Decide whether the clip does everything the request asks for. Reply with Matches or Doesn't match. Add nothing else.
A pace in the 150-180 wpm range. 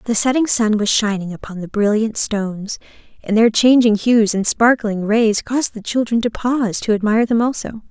Doesn't match